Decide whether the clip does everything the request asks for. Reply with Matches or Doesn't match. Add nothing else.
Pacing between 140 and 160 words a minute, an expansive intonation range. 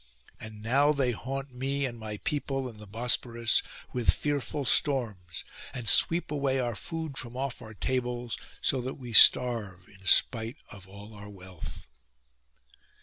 Doesn't match